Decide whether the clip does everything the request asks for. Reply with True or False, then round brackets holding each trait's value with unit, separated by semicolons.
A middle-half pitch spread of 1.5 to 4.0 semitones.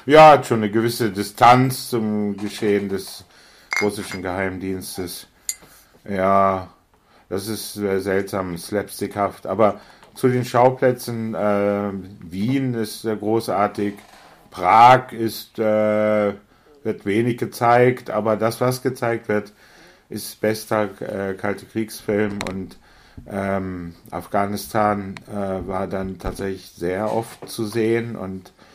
True (2.7 semitones)